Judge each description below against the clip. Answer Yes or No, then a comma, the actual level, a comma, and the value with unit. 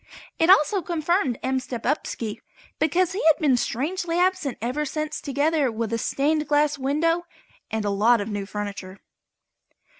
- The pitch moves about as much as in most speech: No, wide, 5.9 semitones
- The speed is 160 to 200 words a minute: No, average, 150 wpm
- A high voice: Yes, very high, 290 Hz